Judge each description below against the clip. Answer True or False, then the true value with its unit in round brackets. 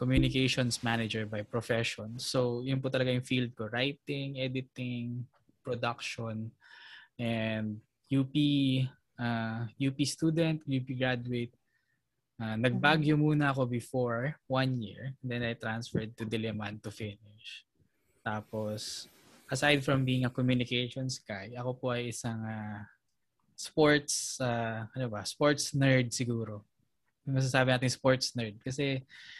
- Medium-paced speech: False (120 wpm)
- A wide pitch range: False (2.7 semitones)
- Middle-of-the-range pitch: False (125 Hz)